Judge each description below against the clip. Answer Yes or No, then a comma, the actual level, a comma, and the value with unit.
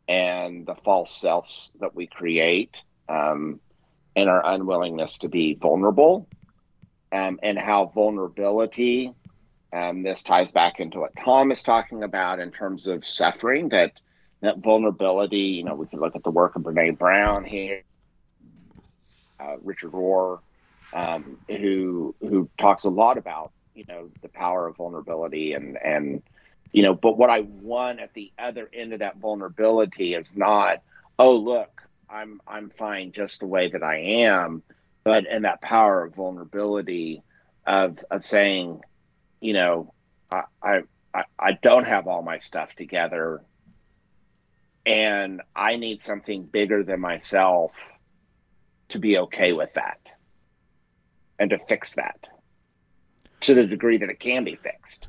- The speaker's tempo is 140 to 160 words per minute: Yes, average, 150 wpm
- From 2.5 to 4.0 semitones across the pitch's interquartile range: Yes, average, 3.7 semitones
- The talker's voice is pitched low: Yes, low, 100 Hz